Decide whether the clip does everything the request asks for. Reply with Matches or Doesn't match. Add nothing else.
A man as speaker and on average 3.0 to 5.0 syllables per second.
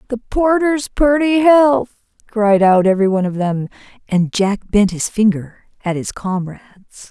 Doesn't match